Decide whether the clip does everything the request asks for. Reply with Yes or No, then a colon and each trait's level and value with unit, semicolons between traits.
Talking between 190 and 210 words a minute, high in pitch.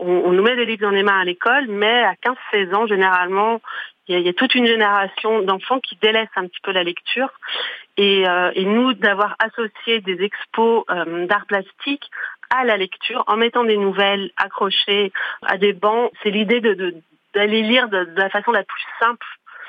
Yes: average, 205 wpm; high, 205 Hz